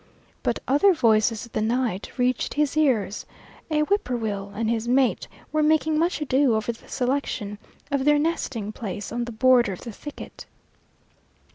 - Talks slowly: No, average, 160 wpm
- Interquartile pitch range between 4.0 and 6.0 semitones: Yes, average, 5.1 semitones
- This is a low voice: No, high, 245 Hz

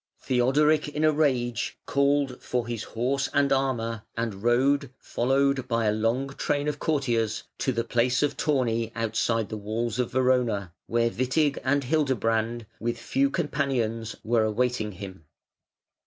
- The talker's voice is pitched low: Yes, low, 125 Hz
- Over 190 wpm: No, average, 145 wpm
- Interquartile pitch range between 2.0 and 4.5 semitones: Yes, average, 3.4 semitones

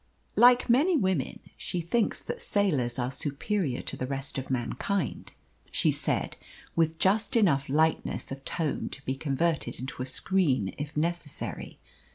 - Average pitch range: No, wide, 6.2 semitones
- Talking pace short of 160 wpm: Yes, average, 150 wpm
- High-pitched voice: No, medium, 155 Hz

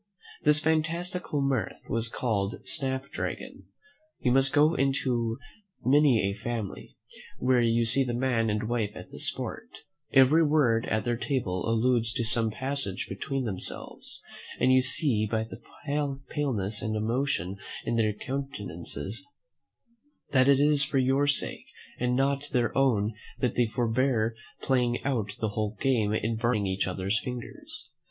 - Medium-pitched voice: No, low, 120 Hz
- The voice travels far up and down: No, average, 3.7 semitones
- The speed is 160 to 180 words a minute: No, average, 145 wpm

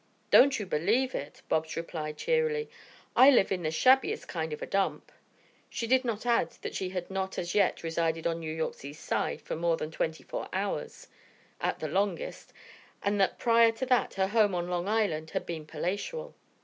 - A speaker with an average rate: Yes, average, 195 wpm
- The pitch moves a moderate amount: No, wide, 6.2 semitones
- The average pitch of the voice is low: No, high, 190 Hz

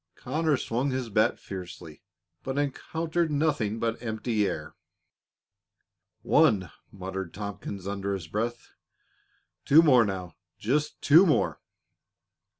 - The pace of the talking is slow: Yes, slow, 110 wpm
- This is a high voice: No, low, 115 Hz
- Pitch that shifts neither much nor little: No, wide, 6.4 semitones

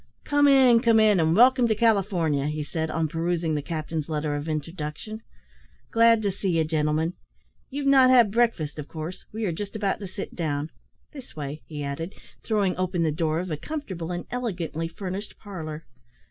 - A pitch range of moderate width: No, wide, 5.7 semitones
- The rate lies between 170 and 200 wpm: Yes, average, 185 wpm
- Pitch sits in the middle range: Yes, medium, 175 Hz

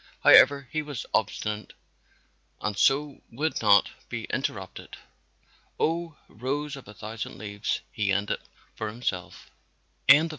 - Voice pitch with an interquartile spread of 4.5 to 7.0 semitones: Yes, wide, 5.6 semitones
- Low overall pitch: Yes, low, 115 Hz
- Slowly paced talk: Yes, slow, 115 wpm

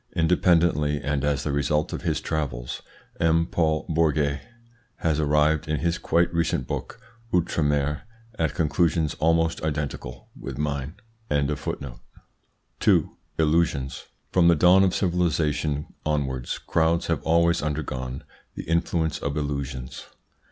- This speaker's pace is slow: Yes, slow, 125 wpm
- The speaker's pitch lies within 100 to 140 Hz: No, very low, 75 Hz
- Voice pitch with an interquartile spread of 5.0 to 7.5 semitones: No, narrow, 2.4 semitones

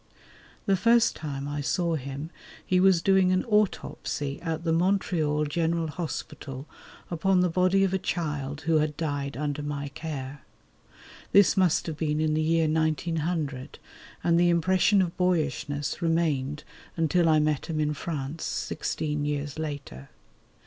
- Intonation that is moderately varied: Yes, average, 3.0 semitones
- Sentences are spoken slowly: No, average, 150 wpm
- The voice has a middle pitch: Yes, medium, 160 Hz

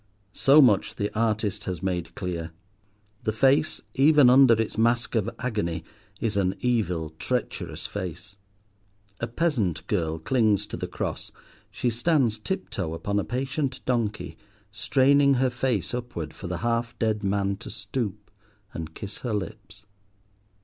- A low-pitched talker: Yes, low, 110 Hz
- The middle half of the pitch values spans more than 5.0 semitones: No, average, 4.5 semitones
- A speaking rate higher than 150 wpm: No, average, 145 wpm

